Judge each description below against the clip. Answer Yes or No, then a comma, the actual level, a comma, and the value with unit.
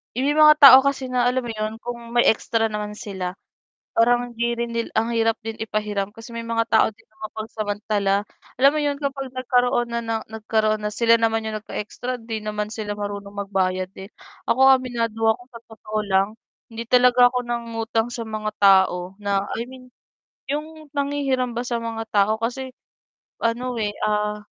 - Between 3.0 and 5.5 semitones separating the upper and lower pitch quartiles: No, narrow, 2.6 semitones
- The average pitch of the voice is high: Yes, high, 225 Hz